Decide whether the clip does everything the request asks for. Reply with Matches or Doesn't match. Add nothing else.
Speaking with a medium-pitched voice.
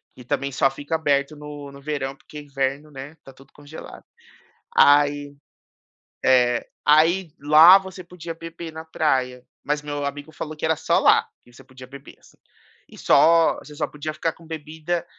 Matches